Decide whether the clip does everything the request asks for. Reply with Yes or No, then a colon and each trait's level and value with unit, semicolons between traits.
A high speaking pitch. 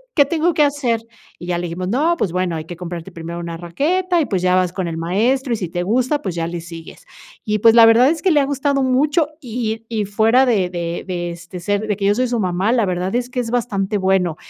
Yes: high, 205 Hz